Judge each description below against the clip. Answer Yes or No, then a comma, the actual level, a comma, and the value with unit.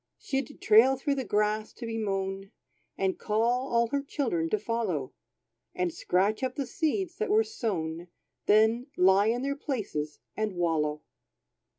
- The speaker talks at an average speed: Yes, average, 155 wpm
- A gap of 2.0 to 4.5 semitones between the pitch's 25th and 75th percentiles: No, wide, 5.5 semitones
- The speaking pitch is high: Yes, high, 215 Hz